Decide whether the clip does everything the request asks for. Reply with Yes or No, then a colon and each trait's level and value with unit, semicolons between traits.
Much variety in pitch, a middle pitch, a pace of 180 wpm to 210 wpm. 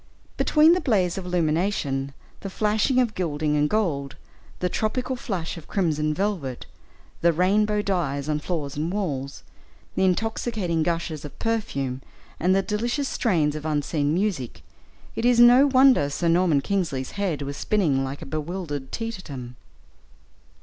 No: wide, 6.2 semitones; medium, 175 Hz; average, 145 wpm